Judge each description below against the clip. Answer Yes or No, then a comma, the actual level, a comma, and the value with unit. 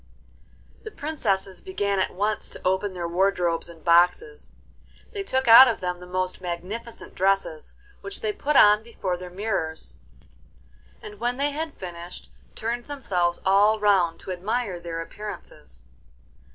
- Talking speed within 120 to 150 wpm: Yes, average, 145 wpm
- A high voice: Yes, high, 195 Hz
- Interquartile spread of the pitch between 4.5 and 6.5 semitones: Yes, average, 4.8 semitones